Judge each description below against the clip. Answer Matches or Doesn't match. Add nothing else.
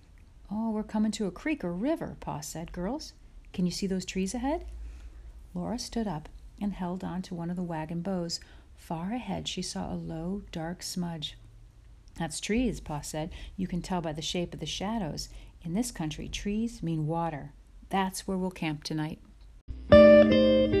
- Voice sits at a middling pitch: Matches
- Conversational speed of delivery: Matches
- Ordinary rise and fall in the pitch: Matches